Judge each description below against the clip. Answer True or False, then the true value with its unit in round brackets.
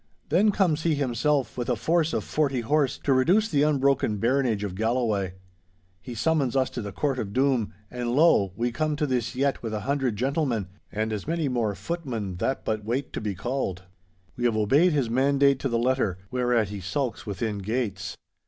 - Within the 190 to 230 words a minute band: True (195 wpm)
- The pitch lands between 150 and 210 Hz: False (125 Hz)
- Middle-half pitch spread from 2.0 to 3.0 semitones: False (4.5 semitones)